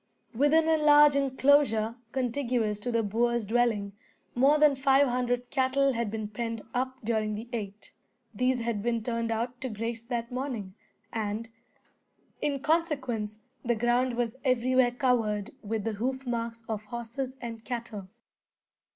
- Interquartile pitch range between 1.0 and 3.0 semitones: Yes, average, 2.7 semitones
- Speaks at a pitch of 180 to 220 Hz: No, high, 240 Hz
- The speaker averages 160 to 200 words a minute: No, average, 145 wpm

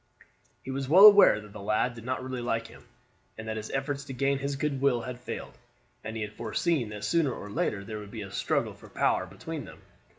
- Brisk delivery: Yes, fast, 235 wpm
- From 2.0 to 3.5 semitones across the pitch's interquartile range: No, average, 4.1 semitones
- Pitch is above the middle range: No, low, 120 Hz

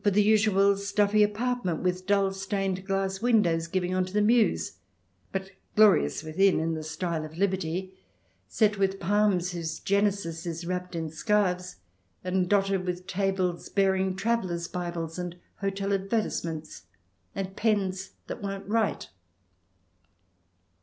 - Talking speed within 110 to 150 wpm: Yes, average, 140 wpm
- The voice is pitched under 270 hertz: Yes, high, 190 Hz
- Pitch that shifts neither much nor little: No, narrow, 2.2 semitones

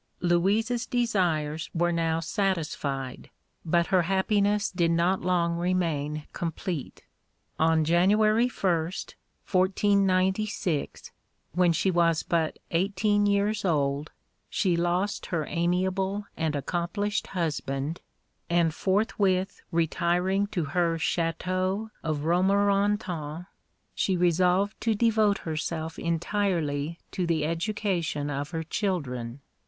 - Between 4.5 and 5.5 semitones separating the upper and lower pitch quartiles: No, average, 3.4 semitones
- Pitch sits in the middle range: Yes, medium, 175 Hz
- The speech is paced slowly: Yes, slow, 105 wpm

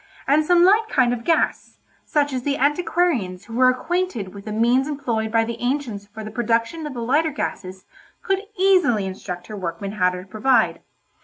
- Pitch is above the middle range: Yes, high, 245 Hz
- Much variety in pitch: Yes, wide, 6.0 semitones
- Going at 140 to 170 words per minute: No, average, 185 wpm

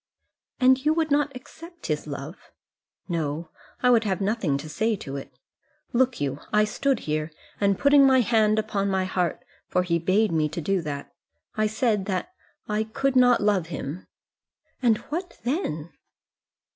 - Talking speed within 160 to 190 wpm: Yes, average, 165 wpm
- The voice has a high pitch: Yes, high, 210 Hz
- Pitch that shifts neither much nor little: No, wide, 7.1 semitones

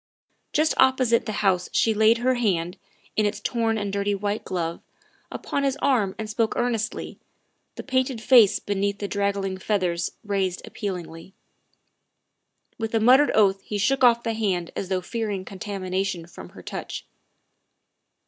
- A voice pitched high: Yes, high, 205 Hz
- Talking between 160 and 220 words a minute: No, average, 150 wpm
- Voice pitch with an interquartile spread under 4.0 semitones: Yes, average, 3.3 semitones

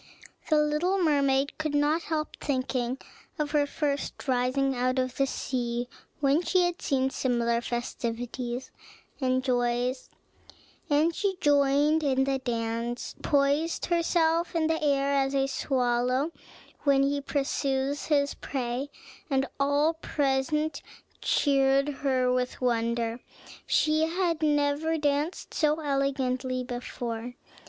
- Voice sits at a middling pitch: No, very high, 275 Hz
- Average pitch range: Yes, average, 3.0 semitones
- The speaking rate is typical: No, slow, 120 wpm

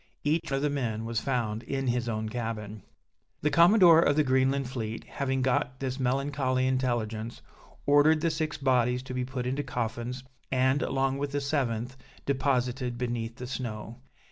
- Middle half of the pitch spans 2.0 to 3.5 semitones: Yes, narrow, 2.6 semitones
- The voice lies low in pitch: Yes, low, 130 Hz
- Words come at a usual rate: Yes, average, 165 wpm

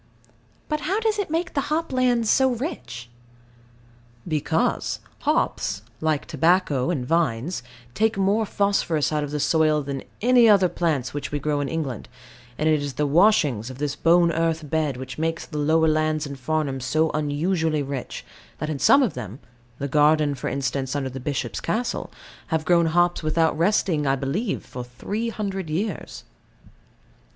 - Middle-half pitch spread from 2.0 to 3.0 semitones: No, average, 5.1 semitones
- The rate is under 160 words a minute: No, average, 165 wpm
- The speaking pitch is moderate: Yes, medium, 155 Hz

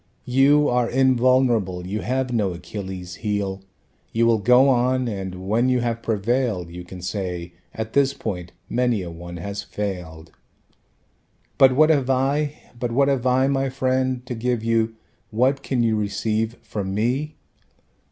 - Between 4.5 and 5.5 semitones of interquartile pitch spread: Yes, average, 4.8 semitones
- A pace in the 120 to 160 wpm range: Yes, average, 155 wpm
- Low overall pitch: Yes, low, 115 Hz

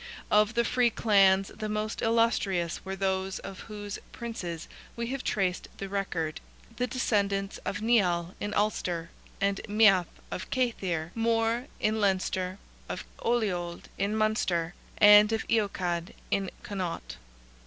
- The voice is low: No, high, 200 Hz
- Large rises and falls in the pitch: No, average, 3.1 semitones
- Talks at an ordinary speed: No, slow, 130 wpm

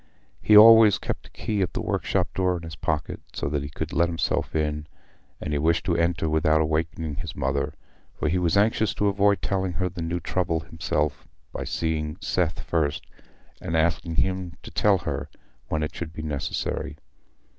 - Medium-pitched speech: No, very low, 80 Hz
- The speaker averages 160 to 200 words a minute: Yes, average, 190 wpm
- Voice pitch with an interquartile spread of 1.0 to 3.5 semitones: Yes, average, 3.0 semitones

